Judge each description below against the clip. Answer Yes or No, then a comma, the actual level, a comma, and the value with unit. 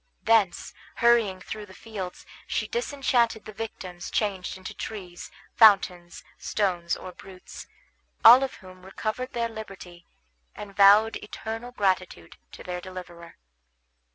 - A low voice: No, high, 200 Hz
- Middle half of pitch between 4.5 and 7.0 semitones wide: No, average, 3.5 semitones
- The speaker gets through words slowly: Yes, slow, 125 wpm